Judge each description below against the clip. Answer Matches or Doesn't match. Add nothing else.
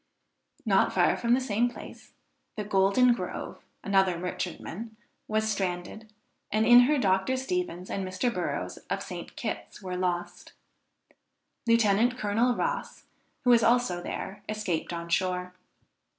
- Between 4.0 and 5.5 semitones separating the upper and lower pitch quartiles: Matches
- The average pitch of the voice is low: Doesn't match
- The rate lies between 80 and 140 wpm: Matches